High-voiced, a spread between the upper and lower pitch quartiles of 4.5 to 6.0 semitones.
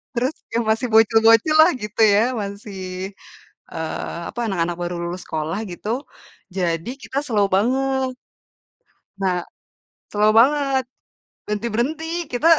Yes: high, 220 Hz; average, 5.0 semitones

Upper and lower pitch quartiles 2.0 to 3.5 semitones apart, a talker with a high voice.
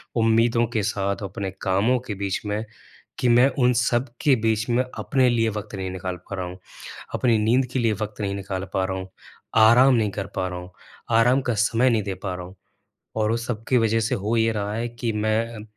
No: average, 3.1 semitones; low, 110 Hz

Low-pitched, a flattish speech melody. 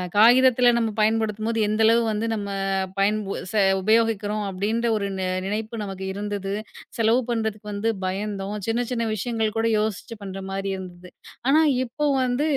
No: high, 215 Hz; narrow, 2.3 semitones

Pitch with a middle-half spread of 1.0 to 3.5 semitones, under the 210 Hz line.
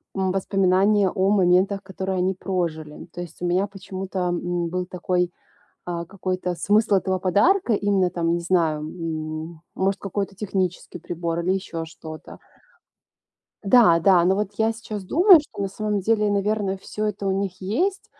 Yes: narrow, 2.4 semitones; high, 190 Hz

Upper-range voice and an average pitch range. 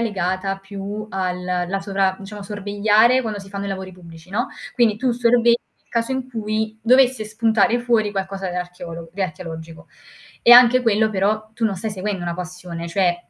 Yes: high, 200 Hz; average, 3.4 semitones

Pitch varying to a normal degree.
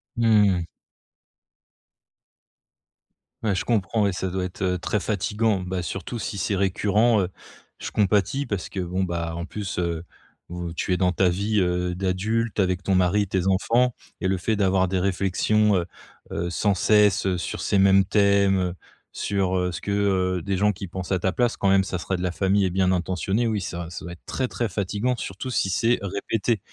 No: narrow, 2.2 semitones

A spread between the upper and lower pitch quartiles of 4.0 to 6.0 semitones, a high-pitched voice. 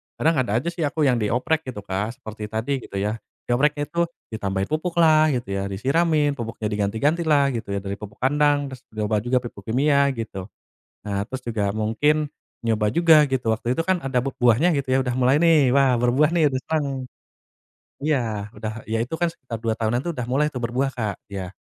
No: average, 5.2 semitones; low, 125 Hz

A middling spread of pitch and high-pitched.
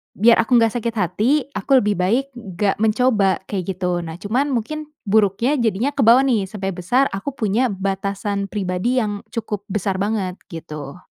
Yes: average, 3.8 semitones; high, 210 Hz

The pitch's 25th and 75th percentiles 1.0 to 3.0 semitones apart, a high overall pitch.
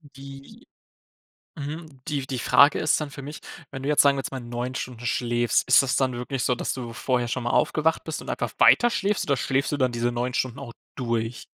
No: average, 2.7 semitones; low, 130 Hz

